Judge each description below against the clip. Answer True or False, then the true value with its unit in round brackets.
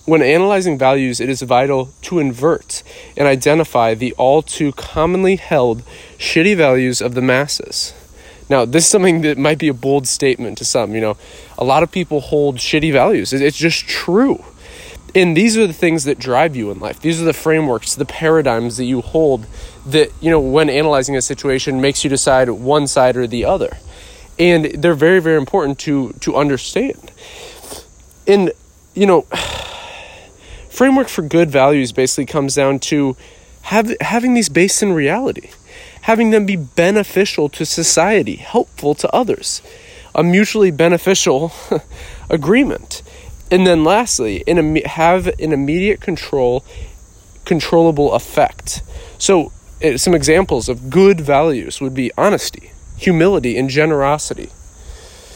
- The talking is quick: False (150 wpm)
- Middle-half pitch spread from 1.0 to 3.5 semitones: False (4.8 semitones)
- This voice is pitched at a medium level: True (150 Hz)